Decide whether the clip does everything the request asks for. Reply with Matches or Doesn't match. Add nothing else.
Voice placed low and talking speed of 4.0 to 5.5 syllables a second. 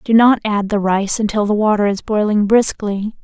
Doesn't match